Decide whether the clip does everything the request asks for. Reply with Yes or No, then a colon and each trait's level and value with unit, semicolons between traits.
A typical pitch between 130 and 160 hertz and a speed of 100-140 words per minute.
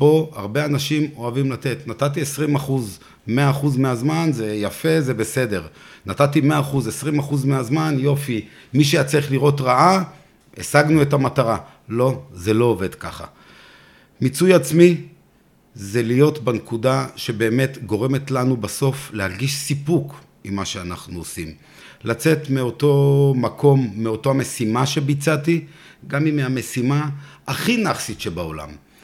Yes: low, 135 Hz; average, 130 wpm